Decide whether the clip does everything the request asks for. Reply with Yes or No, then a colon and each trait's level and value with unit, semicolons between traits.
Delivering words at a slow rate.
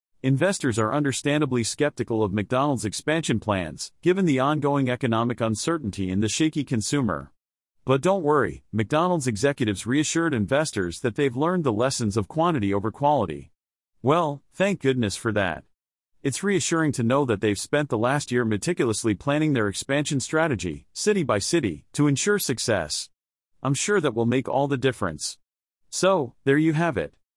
No: average, 160 wpm